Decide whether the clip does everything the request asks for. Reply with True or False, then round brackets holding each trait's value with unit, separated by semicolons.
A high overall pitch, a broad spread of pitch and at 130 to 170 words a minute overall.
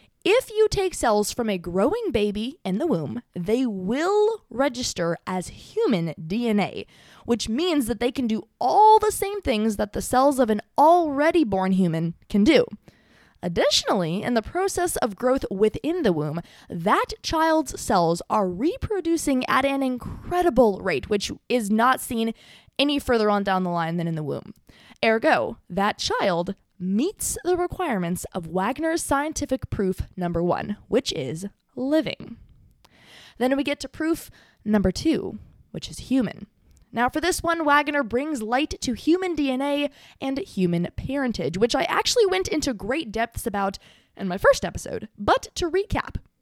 True (250 Hz; 7.9 semitones; 160 wpm)